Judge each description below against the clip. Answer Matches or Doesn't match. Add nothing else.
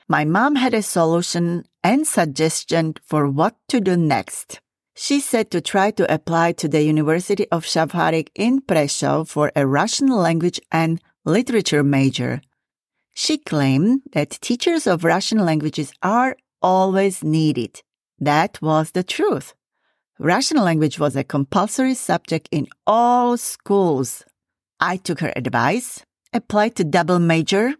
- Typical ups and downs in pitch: Doesn't match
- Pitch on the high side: Doesn't match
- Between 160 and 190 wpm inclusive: Doesn't match